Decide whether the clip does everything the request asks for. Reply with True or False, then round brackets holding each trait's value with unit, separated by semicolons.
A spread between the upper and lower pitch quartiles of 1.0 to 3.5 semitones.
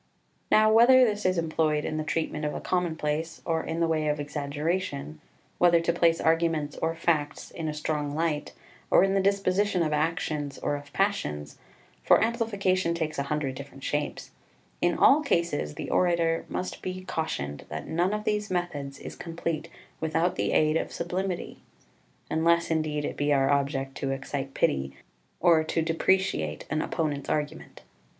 True (3.2 semitones)